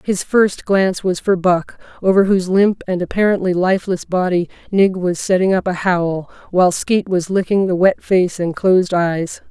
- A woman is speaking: Yes, female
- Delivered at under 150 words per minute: No, average, 185 wpm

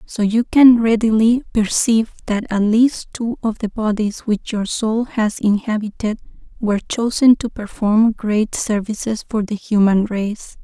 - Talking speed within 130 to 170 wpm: Yes, average, 150 wpm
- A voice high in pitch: Yes, high, 220 Hz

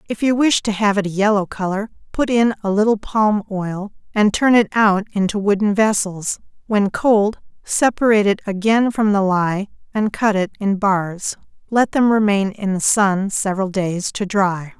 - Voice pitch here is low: No, high, 205 Hz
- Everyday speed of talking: Yes, average, 180 wpm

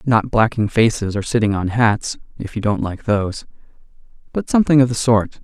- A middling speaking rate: Yes, average, 175 wpm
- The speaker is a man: Yes, male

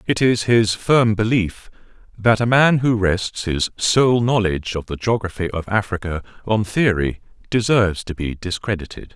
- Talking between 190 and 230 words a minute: No, average, 155 wpm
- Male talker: Yes, male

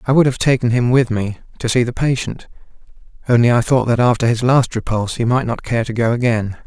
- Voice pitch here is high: No, low, 120 Hz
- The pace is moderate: No, fast, 235 wpm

